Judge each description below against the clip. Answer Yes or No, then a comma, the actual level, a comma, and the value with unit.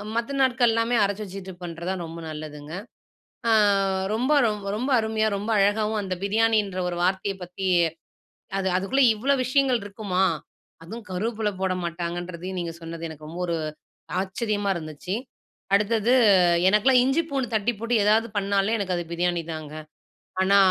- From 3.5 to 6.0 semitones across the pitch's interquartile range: Yes, average, 4.2 semitones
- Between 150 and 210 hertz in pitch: Yes, high, 200 Hz